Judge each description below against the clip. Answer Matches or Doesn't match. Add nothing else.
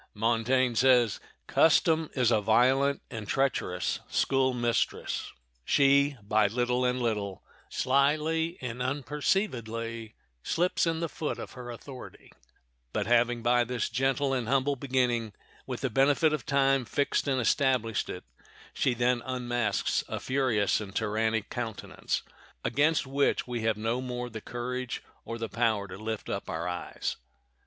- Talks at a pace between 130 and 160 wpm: Matches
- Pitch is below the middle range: Matches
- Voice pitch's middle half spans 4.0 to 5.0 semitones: Doesn't match